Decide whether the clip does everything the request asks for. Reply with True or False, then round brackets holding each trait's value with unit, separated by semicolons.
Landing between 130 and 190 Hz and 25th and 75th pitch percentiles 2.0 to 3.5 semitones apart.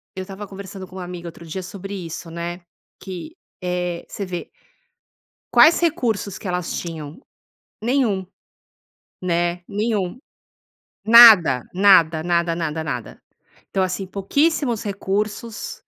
True (185 Hz; 3.2 semitones)